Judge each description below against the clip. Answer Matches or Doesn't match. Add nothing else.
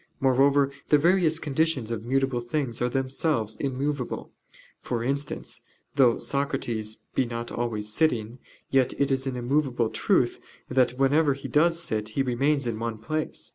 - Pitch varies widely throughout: Doesn't match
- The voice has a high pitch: Doesn't match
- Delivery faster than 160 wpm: Doesn't match